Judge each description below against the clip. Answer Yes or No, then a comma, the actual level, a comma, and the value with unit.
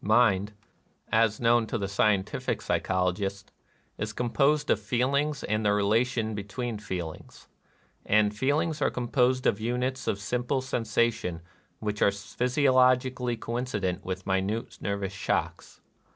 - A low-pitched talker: Yes, low, 110 Hz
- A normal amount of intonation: Yes, average, 3.9 semitones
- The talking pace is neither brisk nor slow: No, slow, 130 wpm